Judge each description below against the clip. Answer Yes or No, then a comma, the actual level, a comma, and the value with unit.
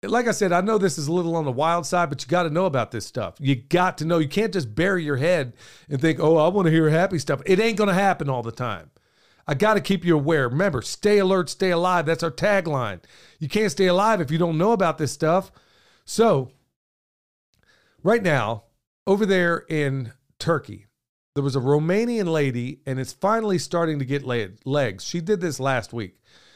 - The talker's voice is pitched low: No, medium, 160 Hz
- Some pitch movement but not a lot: No, wide, 5.8 semitones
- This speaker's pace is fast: Yes, fast, 220 wpm